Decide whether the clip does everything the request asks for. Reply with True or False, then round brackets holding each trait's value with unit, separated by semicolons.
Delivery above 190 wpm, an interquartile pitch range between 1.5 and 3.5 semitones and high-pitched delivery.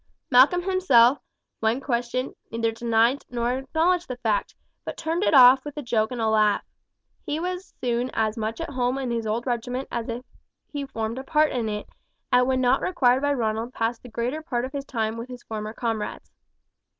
True (200 wpm; 3.1 semitones; 245 Hz)